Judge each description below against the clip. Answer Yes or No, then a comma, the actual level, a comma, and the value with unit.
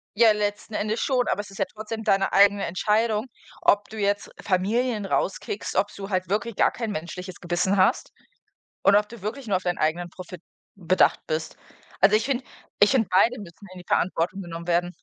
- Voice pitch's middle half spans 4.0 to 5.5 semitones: No, average, 2.9 semitones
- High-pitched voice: Yes, high, 200 Hz